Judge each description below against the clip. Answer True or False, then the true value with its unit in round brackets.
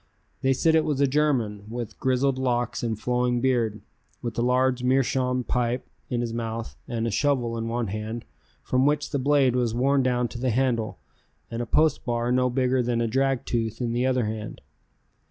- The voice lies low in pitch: True (125 Hz)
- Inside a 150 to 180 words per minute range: False (195 wpm)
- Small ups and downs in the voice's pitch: True (2.0 semitones)